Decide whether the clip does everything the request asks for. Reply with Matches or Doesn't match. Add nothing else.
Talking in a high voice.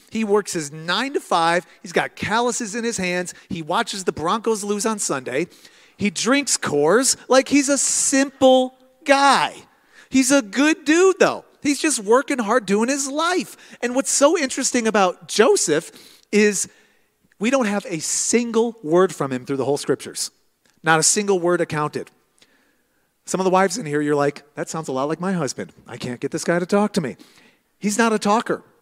Matches